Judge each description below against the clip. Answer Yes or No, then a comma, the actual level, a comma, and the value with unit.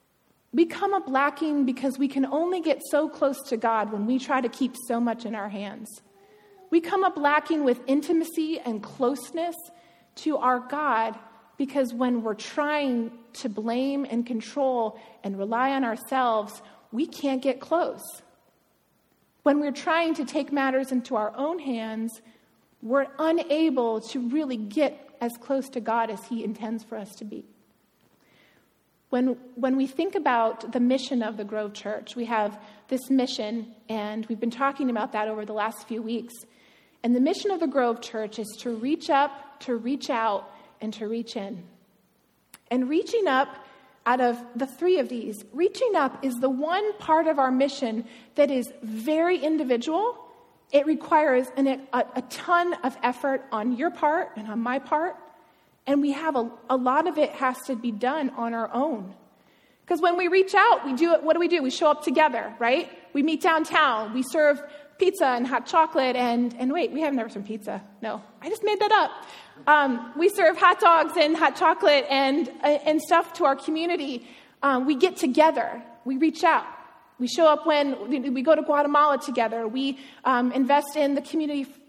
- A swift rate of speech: No, average, 180 wpm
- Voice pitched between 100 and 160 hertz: No, very high, 270 Hz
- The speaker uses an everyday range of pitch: Yes, average, 4.8 semitones